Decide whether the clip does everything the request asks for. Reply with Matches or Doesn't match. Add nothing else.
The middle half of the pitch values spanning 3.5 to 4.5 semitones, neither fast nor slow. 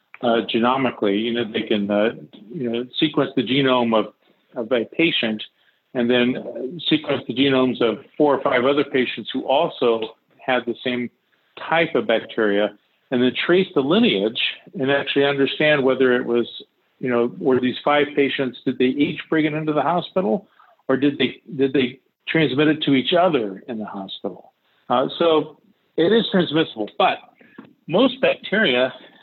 Matches